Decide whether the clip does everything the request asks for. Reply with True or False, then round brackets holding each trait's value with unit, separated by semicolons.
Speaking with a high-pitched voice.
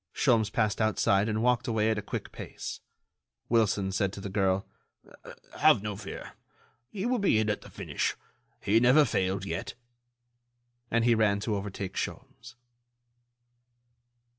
False (110 Hz)